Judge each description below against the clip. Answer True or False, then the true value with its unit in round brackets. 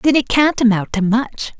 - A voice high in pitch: True (240 Hz)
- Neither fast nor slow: False (225 wpm)